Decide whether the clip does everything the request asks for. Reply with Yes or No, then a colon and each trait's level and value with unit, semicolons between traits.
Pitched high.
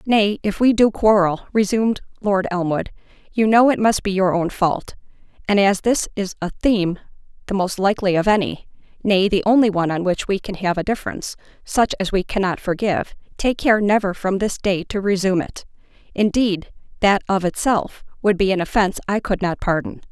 Yes: high, 200 Hz